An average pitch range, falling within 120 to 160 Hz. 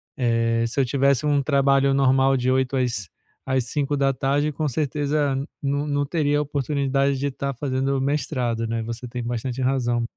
No: narrow, 2.3 semitones; low, 135 Hz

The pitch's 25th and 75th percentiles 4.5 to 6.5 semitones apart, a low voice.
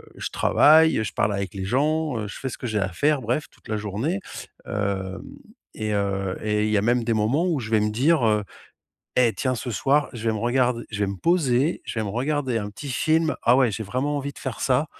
Yes: average, 5.2 semitones; low, 120 Hz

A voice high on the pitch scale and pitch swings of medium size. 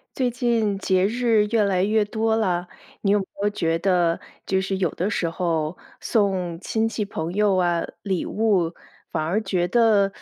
Yes: high, 195 Hz; average, 3.5 semitones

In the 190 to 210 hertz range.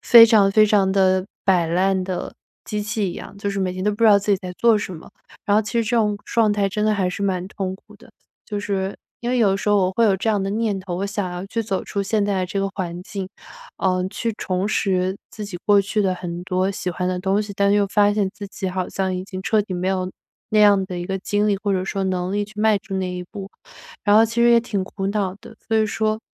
Yes: high, 200 Hz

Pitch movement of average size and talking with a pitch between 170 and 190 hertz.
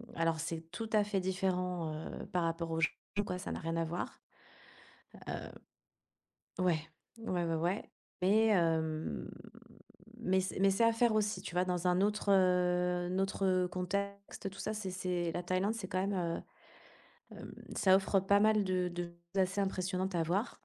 No: narrow, 2.0 semitones; medium, 185 Hz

